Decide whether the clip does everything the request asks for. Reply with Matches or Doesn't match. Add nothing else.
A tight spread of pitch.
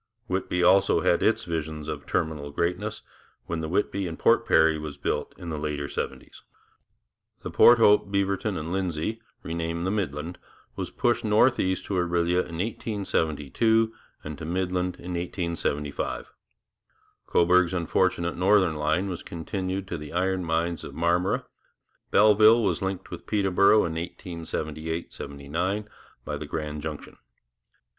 Doesn't match